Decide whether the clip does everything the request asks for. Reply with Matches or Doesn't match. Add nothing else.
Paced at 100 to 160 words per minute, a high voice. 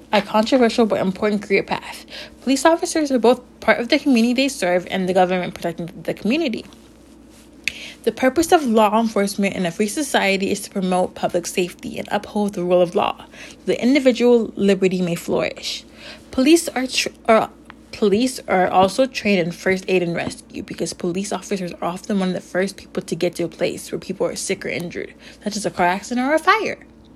Doesn't match